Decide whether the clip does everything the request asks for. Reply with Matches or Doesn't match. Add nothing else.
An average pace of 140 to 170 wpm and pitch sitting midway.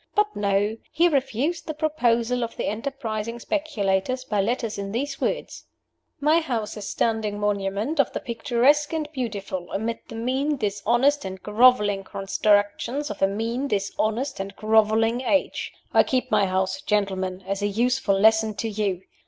Doesn't match